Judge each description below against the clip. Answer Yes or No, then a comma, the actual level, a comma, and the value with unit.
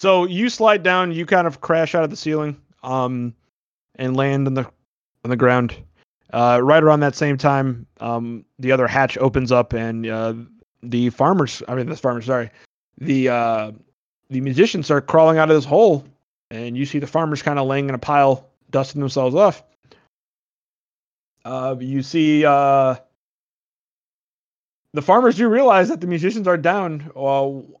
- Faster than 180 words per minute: No, average, 170 wpm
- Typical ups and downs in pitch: Yes, average, 3.8 semitones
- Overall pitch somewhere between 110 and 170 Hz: Yes, low, 135 Hz